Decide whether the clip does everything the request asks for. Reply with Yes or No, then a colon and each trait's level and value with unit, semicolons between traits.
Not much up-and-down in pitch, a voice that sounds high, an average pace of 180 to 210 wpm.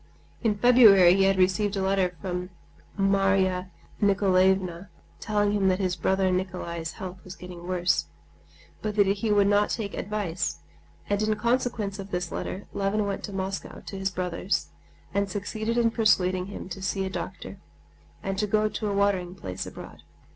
No: narrow, 2.0 semitones; high, 195 Hz; average, 170 wpm